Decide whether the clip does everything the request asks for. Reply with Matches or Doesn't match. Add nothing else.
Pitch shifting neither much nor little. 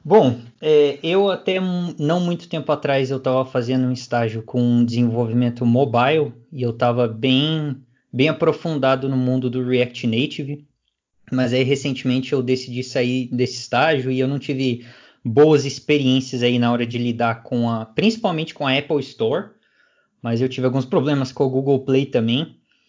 Matches